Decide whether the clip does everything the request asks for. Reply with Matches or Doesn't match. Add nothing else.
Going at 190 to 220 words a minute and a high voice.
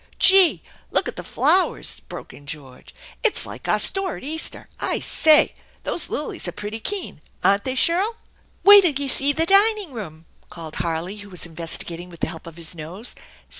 Doesn't match